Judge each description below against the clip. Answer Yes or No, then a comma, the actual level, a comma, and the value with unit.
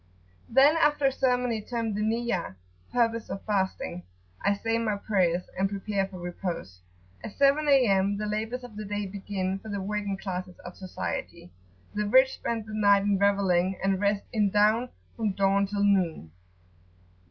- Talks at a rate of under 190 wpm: Yes, average, 165 wpm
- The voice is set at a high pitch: Yes, high, 205 Hz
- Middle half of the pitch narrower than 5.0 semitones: Yes, average, 2.8 semitones